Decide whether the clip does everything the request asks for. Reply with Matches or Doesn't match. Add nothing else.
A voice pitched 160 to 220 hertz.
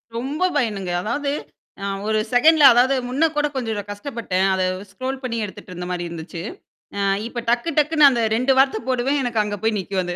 Doesn't match